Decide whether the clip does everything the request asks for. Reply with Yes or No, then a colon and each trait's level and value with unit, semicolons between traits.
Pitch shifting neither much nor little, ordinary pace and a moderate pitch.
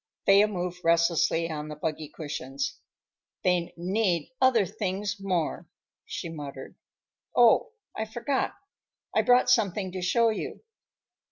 No: average, 4.4 semitones; slow, 120 wpm; medium, 180 Hz